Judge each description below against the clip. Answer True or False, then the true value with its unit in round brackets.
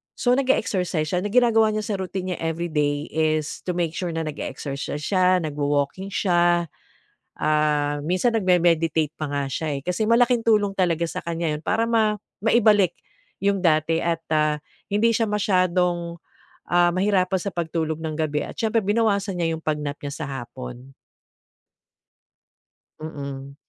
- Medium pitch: True (170 Hz)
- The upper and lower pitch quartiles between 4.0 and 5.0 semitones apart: True (4.6 semitones)